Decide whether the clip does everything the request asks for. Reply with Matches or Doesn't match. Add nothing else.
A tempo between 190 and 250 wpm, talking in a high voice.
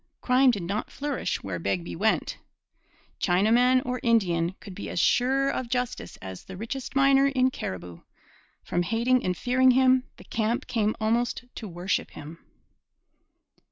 Doesn't match